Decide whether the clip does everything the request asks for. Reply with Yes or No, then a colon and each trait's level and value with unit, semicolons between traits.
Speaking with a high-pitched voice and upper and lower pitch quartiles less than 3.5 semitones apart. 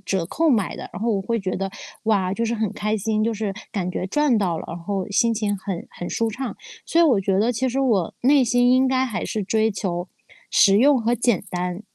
No: high, 215 Hz; average, 3.9 semitones